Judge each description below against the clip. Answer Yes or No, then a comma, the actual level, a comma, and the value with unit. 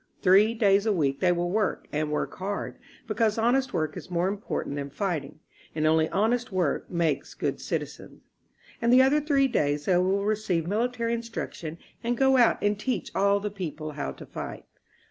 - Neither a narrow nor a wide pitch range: No, wide, 6.1 semitones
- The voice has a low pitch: No, high, 200 Hz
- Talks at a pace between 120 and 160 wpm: No, average, 185 wpm